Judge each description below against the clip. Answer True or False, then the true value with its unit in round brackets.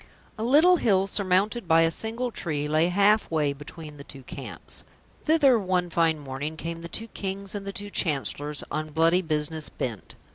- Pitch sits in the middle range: True (170 Hz)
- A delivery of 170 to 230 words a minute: True (180 wpm)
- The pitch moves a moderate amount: True (4.9 semitones)